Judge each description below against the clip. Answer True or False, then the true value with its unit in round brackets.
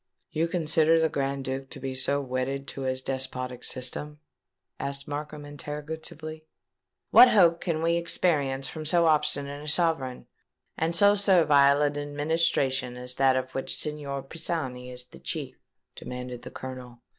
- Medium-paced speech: True (150 wpm)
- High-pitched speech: False (145 Hz)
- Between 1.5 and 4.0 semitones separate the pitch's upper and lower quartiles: True (3.3 semitones)